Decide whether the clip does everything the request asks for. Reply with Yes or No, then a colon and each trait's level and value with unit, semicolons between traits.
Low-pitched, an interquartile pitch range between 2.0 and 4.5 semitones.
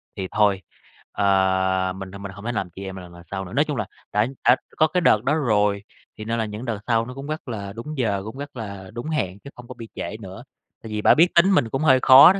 No: low, 110 Hz; average, 5.1 semitones